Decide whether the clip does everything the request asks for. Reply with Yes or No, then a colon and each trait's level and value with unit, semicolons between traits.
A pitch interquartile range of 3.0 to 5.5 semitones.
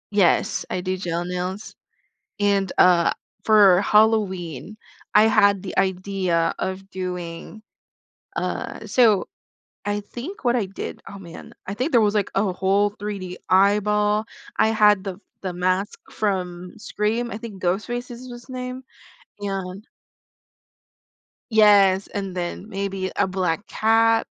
No: narrow, 2.5 semitones